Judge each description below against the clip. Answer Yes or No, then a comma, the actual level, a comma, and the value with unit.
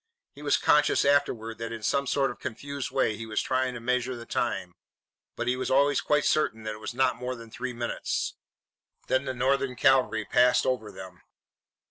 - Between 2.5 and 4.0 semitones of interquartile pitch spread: Yes, average, 2.8 semitones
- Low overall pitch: Yes, low, 125 Hz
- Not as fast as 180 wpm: No, average, 195 wpm